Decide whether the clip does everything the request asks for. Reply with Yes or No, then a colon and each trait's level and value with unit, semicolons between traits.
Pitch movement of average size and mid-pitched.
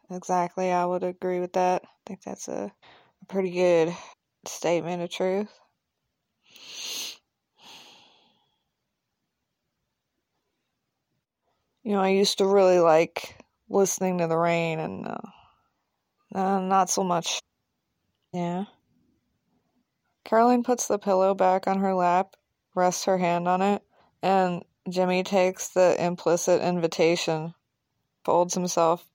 No: narrow, 1.9 semitones; medium, 180 Hz